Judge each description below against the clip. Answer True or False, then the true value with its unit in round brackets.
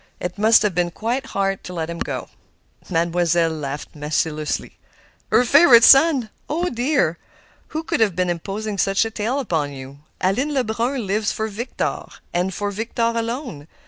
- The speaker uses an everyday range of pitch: False (5.7 semitones)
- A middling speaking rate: True (160 wpm)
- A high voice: True (205 Hz)